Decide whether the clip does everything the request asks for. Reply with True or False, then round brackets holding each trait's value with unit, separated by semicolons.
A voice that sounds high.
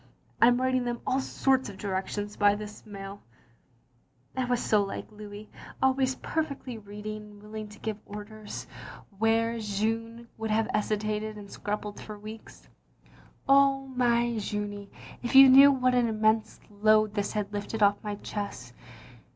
True (215 Hz)